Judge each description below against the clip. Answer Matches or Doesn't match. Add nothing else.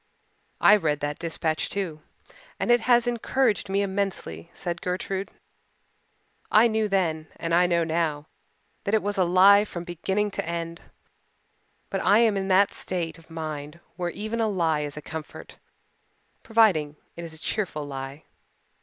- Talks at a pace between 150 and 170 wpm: Matches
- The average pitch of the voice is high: Doesn't match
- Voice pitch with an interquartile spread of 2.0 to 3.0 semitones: Doesn't match